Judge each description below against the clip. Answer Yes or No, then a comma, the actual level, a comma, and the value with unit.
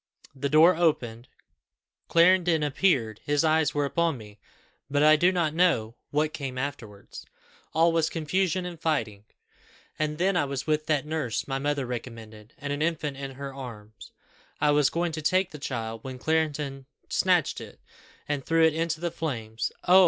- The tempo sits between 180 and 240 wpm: No, average, 170 wpm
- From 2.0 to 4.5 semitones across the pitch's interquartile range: Yes, average, 3.9 semitones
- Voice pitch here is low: No, medium, 150 Hz